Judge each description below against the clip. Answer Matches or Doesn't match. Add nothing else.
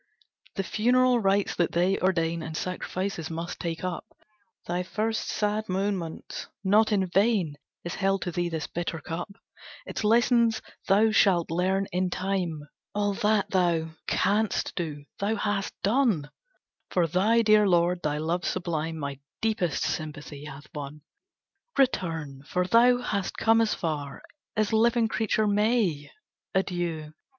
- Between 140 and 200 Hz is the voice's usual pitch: Matches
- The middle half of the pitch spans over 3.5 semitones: Matches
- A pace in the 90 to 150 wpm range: Matches